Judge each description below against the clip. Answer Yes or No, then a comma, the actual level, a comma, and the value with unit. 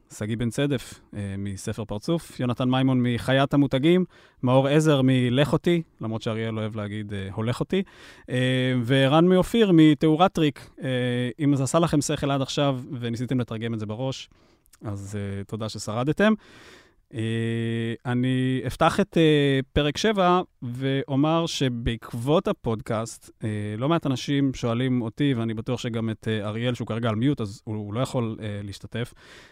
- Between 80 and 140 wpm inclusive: Yes, average, 135 wpm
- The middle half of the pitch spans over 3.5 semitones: Yes, average, 4.4 semitones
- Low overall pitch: Yes, low, 125 Hz